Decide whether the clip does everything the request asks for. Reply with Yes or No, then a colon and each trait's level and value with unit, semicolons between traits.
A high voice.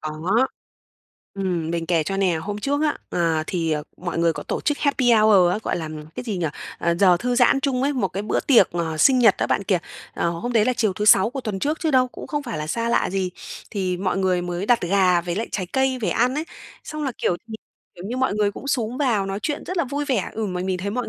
Yes: high, 205 Hz